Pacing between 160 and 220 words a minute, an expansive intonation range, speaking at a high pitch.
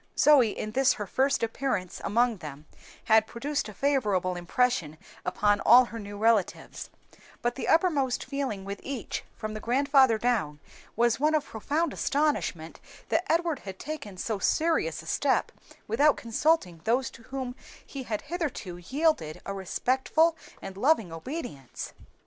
No: average, 150 wpm; wide, 5.8 semitones; high, 240 Hz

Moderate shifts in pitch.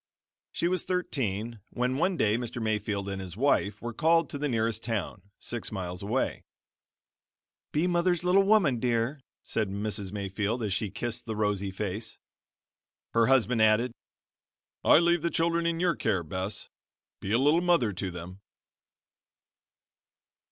No: wide, 6.7 semitones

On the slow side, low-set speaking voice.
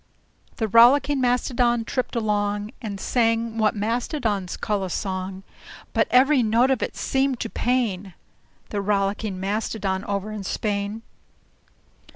No: slow, 130 wpm; high, 220 Hz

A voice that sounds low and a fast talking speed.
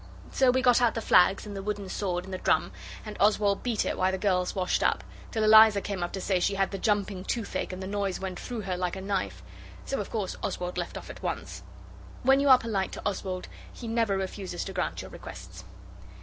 No: high, 200 Hz; fast, 235 wpm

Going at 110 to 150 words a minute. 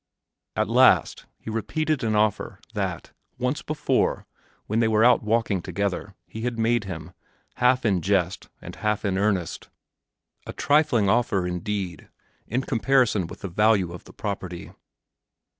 Yes: average, 145 wpm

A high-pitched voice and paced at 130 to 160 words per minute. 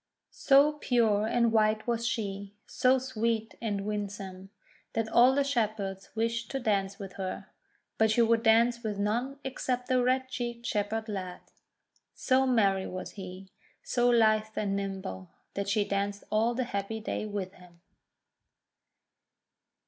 Yes: high, 220 Hz; average, 150 wpm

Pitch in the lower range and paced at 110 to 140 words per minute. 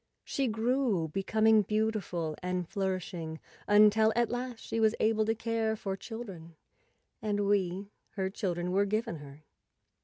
No: high, 205 Hz; slow, 135 wpm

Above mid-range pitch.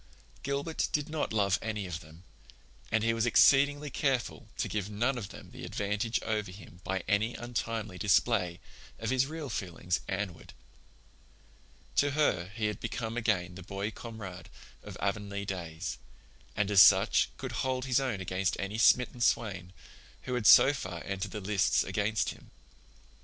No: low, 105 Hz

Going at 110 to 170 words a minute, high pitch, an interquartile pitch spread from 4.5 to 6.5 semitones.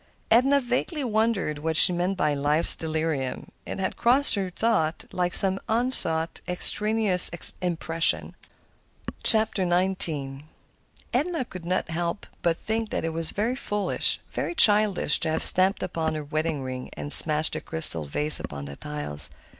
No: average, 145 wpm; medium, 175 Hz; wide, 5.5 semitones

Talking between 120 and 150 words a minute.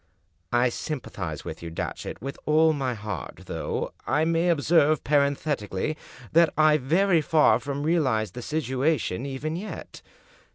Yes: average, 140 wpm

